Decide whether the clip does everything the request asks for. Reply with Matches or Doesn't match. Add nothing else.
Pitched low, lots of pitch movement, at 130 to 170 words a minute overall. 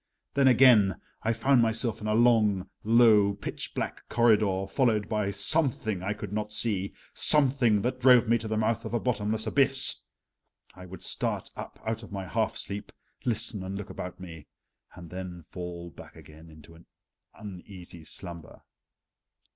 Doesn't match